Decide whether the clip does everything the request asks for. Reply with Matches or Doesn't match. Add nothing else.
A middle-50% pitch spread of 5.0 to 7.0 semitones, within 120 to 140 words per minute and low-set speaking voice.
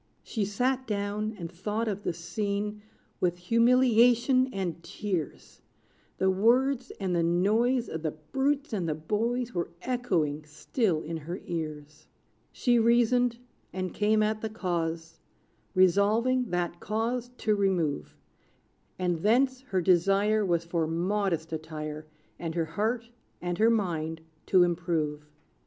Doesn't match